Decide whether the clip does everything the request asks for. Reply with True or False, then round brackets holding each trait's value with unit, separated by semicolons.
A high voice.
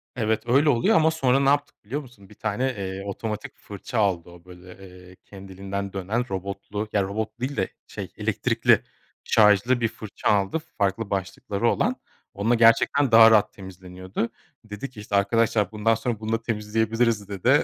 False (105 Hz)